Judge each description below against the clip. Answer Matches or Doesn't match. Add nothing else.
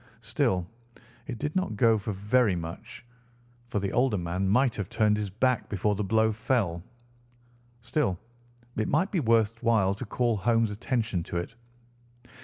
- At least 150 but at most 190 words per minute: Matches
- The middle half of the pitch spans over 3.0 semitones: Matches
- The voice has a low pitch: Matches